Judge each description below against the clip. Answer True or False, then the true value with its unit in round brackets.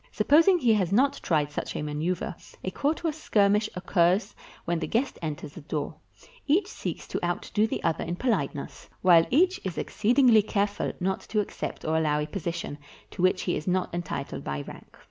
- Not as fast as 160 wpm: False (185 wpm)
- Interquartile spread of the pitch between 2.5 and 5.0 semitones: False (5.6 semitones)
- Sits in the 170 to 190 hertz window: True (185 Hz)